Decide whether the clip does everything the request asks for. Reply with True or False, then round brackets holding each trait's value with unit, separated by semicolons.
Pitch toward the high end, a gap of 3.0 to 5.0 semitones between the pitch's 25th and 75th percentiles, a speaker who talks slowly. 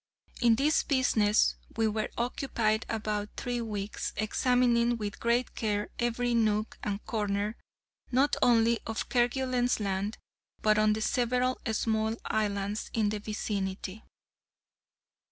False (220 Hz; 2.4 semitones; 120 wpm)